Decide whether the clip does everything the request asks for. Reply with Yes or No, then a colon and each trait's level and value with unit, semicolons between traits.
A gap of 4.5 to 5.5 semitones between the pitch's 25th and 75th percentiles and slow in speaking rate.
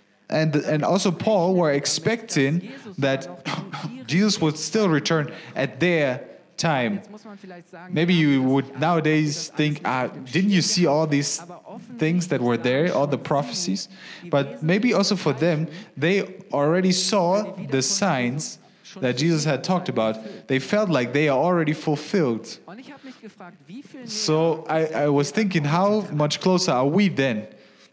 No: average, 4.8 semitones; average, 140 wpm